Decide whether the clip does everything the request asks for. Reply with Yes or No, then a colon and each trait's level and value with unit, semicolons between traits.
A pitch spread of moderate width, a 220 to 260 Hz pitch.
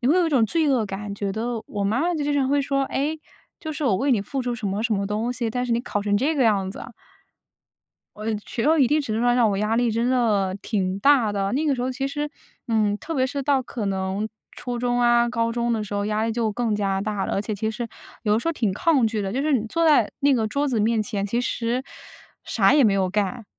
Yes: average, 4.3 semitones; high, 230 Hz